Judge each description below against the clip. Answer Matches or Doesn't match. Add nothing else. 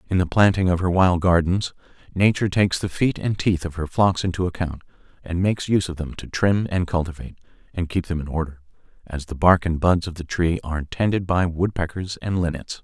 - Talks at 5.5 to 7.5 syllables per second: Matches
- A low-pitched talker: Matches